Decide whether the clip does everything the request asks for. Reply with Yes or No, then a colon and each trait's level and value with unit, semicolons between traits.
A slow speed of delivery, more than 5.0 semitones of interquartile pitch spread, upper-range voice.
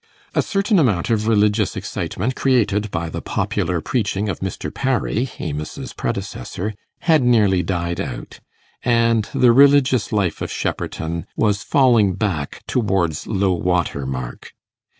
No: slow, 130 wpm; wide, 5.4 semitones; low, 105 Hz